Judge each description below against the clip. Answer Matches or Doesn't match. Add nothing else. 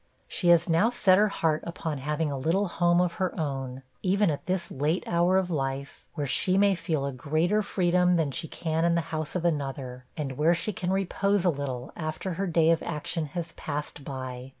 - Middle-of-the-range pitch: Matches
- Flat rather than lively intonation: Doesn't match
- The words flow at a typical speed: Doesn't match